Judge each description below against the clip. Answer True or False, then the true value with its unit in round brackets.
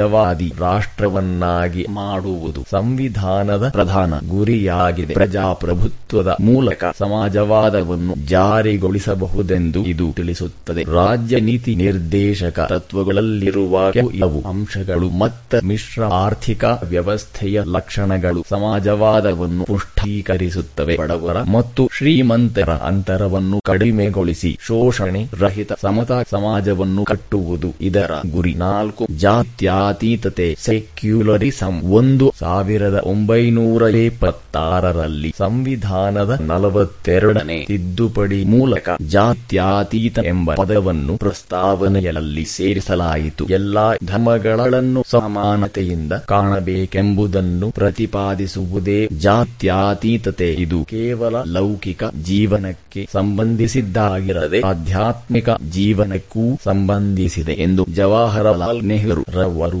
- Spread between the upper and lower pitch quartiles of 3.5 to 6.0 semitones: False (3.0 semitones)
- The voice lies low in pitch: True (100 Hz)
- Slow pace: True (65 wpm)